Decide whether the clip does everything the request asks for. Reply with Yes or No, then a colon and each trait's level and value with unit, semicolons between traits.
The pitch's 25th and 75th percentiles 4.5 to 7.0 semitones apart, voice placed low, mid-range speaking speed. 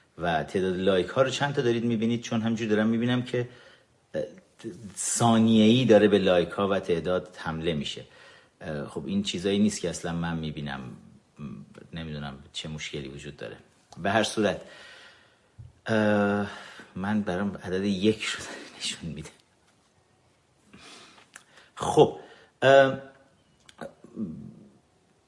Yes: wide, 5.5 semitones; low, 105 Hz; average, 115 wpm